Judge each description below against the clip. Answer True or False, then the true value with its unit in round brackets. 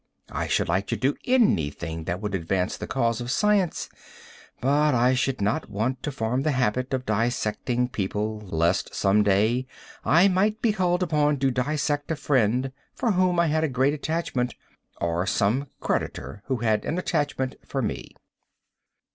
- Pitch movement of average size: False (6.0 semitones)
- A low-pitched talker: True (130 Hz)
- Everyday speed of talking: True (165 wpm)